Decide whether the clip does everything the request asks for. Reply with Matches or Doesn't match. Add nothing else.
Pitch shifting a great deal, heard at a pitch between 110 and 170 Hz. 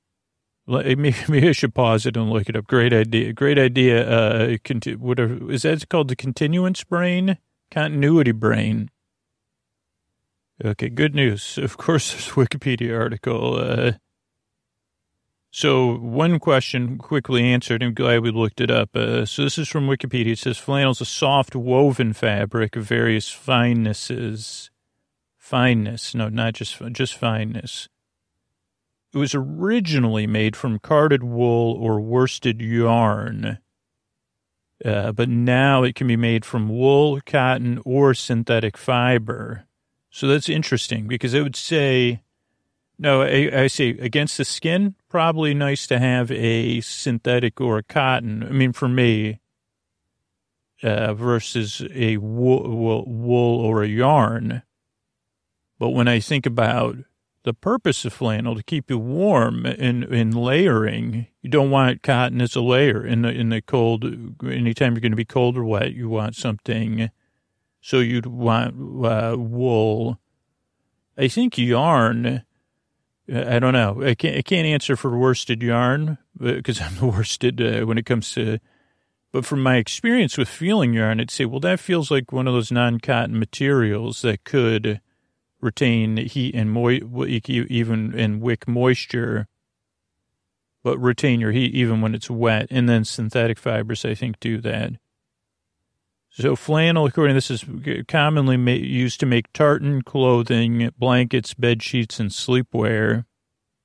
Doesn't match